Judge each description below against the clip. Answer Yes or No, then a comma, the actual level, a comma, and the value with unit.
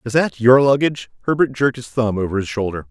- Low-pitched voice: Yes, low, 120 Hz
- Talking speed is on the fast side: Yes, fast, 230 wpm